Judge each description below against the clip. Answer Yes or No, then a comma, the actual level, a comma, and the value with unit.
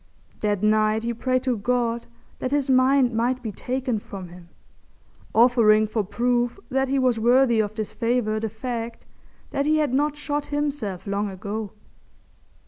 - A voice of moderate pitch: No, high, 235 Hz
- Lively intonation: No, average, 3.2 semitones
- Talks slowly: No, average, 160 wpm